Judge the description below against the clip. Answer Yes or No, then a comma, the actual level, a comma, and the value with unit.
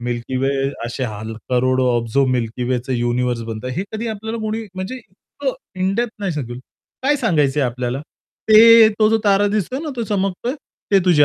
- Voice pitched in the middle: Yes, medium, 150 Hz